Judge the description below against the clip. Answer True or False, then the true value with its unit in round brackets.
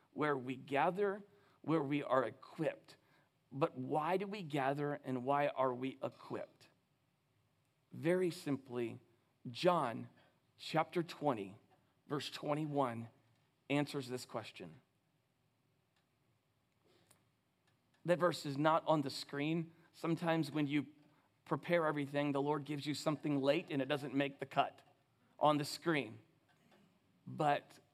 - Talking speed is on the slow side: True (120 wpm)